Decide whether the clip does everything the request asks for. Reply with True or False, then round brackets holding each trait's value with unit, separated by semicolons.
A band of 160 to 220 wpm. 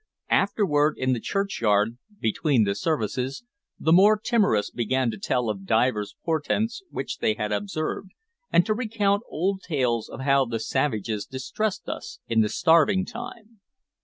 False (150 wpm)